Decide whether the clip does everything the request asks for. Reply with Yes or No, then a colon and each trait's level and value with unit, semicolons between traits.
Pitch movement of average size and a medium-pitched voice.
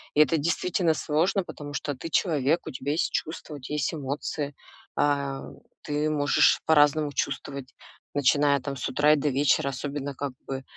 No: narrow, 1.7 semitones; medium, 145 Hz